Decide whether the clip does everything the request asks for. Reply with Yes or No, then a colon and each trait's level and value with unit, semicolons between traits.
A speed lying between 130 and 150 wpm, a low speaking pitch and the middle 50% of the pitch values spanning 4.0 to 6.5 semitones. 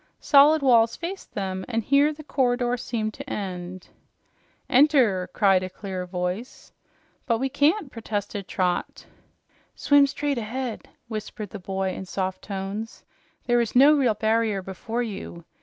No: average, 140 wpm; high, 225 Hz; wide, 5.4 semitones